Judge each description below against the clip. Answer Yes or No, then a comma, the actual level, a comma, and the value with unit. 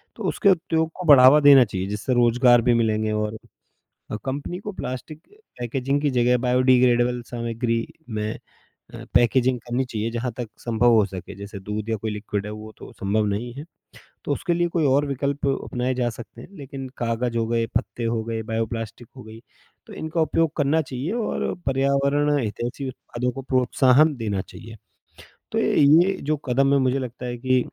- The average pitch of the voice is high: No, low, 125 Hz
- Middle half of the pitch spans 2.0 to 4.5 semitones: Yes, average, 3.5 semitones